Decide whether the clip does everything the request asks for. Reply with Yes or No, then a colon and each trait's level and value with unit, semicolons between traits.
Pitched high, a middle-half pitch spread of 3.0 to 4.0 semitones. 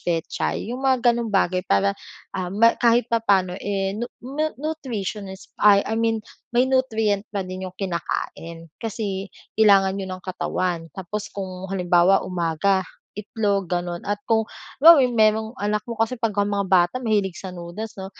Yes: high, 200 Hz; average, 3.4 semitones